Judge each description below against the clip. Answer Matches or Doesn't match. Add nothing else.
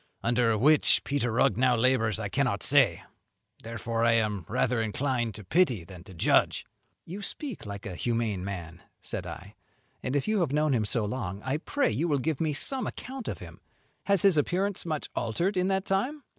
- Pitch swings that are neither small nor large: Doesn't match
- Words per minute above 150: Matches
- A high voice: Doesn't match